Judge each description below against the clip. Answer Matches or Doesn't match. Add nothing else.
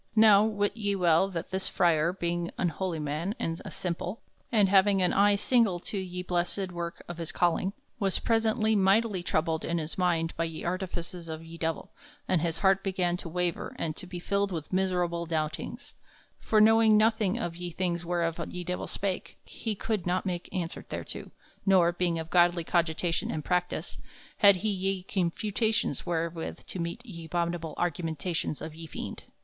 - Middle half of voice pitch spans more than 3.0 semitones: Doesn't match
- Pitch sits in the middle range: Matches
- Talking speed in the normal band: Matches